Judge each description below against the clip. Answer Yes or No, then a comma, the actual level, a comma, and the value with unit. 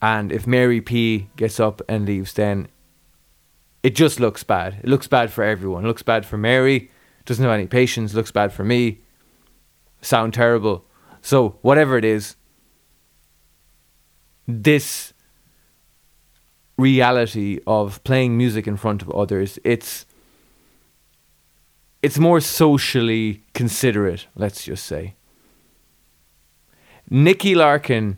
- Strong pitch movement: Yes, wide, 7.7 semitones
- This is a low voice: Yes, low, 110 Hz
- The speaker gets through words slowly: Yes, slow, 115 wpm